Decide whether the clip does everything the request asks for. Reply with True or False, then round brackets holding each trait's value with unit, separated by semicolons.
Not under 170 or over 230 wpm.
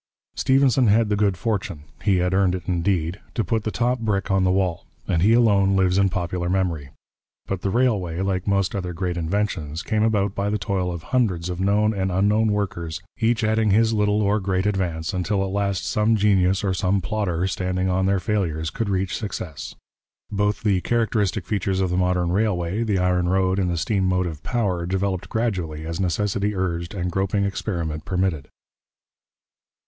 True (185 wpm)